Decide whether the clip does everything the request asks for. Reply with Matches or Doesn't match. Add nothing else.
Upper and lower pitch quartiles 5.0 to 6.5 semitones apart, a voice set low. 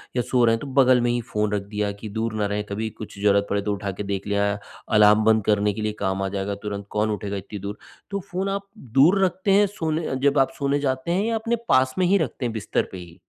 Matches